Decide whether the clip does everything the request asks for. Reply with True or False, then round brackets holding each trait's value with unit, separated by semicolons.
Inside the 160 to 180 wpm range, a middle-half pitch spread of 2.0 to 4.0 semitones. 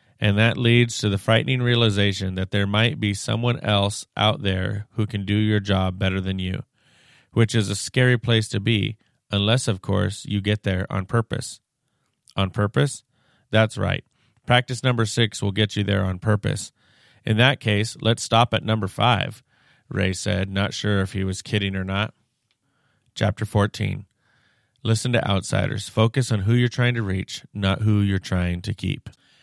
True (175 wpm; 3.1 semitones)